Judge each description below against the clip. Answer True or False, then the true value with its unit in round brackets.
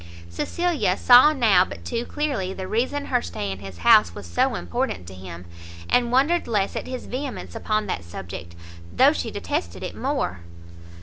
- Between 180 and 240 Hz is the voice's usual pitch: True (190 Hz)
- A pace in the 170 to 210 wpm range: True (175 wpm)